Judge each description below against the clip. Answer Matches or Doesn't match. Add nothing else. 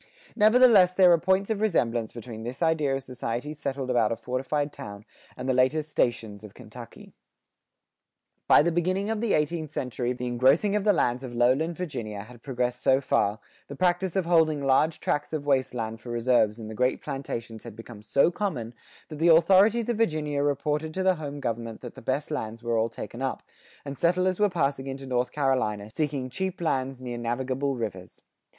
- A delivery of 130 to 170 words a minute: Doesn't match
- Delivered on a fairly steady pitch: Doesn't match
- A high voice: Doesn't match